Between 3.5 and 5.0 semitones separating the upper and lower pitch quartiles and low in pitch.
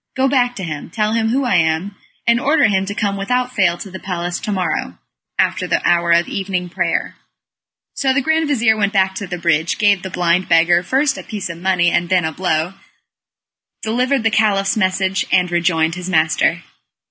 No: average, 4.3 semitones; high, 190 Hz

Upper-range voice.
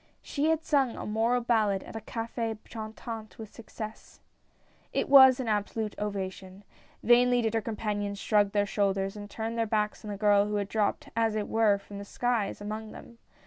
Yes: high, 215 Hz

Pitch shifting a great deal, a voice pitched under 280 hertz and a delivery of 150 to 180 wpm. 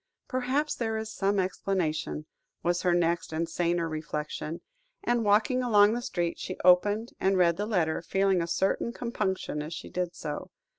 No: average, 4.3 semitones; medium, 185 Hz; average, 165 wpm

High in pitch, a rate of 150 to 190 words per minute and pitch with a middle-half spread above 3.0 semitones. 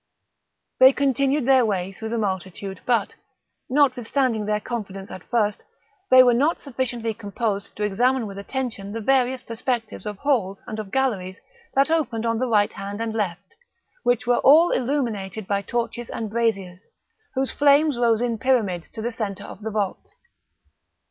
Yes: high, 230 Hz; average, 160 wpm; average, 4.2 semitones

